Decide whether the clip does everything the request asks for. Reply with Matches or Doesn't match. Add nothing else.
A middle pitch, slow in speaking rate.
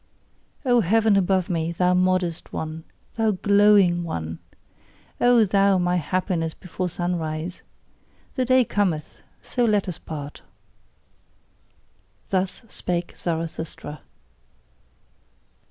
Matches